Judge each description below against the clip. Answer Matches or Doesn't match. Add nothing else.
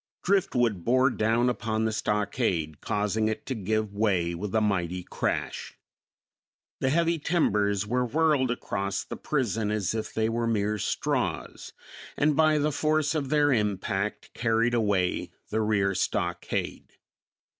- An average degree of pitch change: Matches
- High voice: Doesn't match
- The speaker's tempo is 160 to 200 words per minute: Doesn't match